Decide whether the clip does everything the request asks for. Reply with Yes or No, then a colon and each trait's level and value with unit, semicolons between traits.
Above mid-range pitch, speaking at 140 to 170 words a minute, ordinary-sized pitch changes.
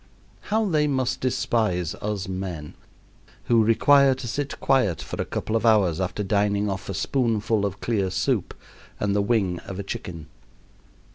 No: low, 105 Hz; average, 160 wpm; average, 4.0 semitones